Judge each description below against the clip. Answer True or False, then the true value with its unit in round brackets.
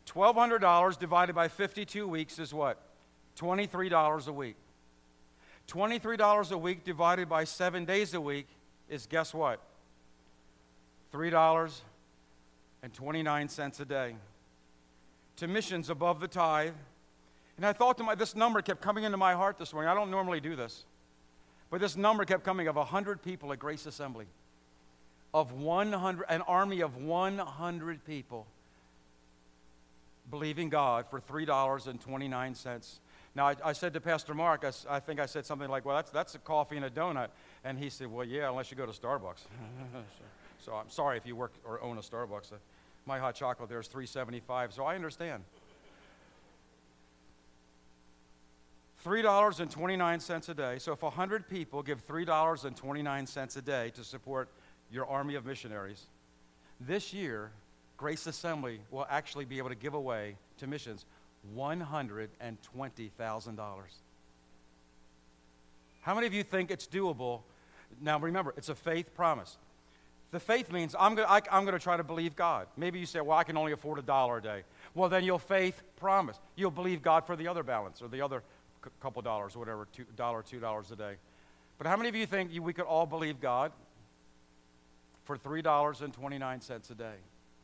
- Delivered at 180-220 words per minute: False (165 wpm)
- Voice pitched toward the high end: False (140 Hz)